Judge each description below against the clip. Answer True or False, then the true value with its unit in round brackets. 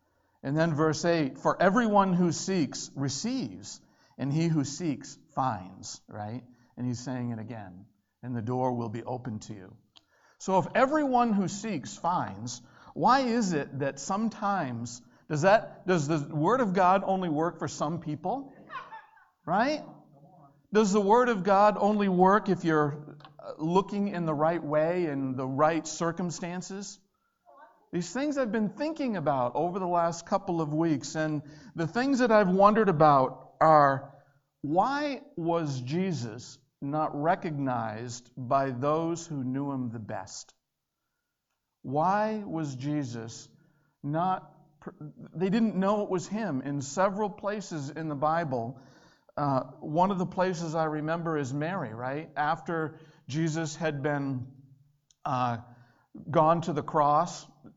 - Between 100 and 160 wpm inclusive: True (140 wpm)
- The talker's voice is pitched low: False (160 Hz)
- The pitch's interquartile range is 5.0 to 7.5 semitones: True (5.3 semitones)